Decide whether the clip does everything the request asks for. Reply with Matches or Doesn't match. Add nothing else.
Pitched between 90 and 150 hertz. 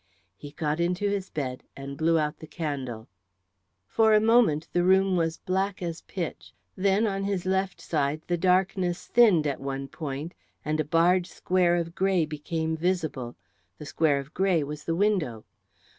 Doesn't match